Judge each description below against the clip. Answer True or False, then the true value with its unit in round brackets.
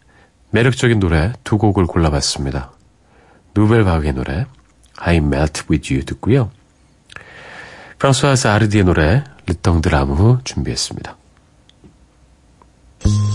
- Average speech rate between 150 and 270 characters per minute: False (295 characters per minute)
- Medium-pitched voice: False (85 Hz)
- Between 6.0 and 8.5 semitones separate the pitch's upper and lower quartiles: True (6.9 semitones)